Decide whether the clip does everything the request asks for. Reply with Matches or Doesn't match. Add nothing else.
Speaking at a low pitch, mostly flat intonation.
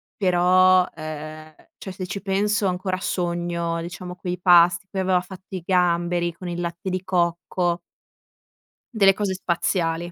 Doesn't match